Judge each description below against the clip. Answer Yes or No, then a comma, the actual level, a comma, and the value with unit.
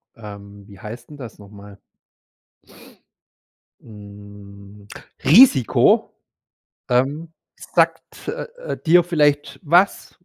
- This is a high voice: No, low, 110 Hz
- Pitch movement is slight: No, wide, 6.5 semitones